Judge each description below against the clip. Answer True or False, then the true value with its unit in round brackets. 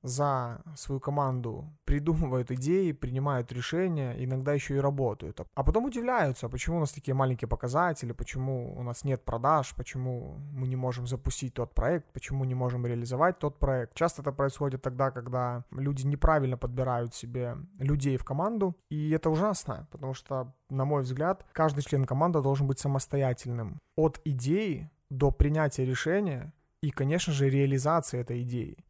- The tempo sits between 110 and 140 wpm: False (155 wpm)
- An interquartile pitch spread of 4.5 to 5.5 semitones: False (3.3 semitones)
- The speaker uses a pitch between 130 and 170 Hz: True (135 Hz)